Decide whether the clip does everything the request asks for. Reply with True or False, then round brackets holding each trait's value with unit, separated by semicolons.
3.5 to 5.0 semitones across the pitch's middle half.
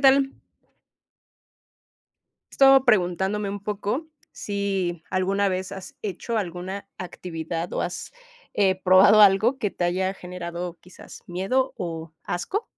False (2.8 semitones)